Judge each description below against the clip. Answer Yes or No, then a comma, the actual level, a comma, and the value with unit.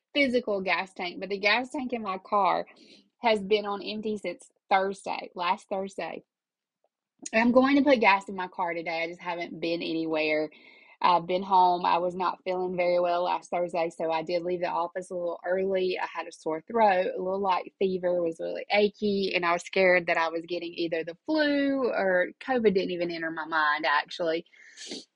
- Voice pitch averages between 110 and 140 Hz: No, medium, 180 Hz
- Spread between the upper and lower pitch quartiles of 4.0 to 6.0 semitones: No, average, 3.2 semitones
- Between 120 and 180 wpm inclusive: No, average, 200 wpm